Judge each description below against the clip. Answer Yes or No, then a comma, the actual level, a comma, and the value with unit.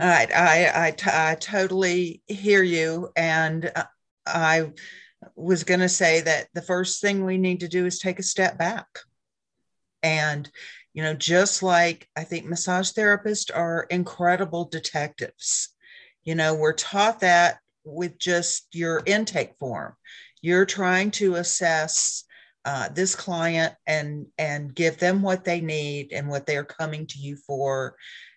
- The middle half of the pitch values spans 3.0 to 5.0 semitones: No, narrow, 2.6 semitones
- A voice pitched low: No, medium, 170 Hz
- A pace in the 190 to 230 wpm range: No, average, 150 wpm